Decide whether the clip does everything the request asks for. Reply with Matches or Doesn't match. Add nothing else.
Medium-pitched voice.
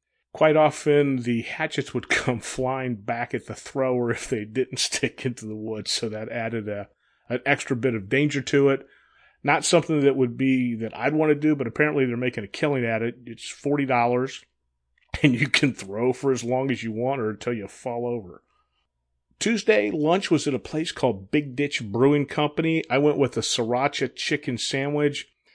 Doesn't match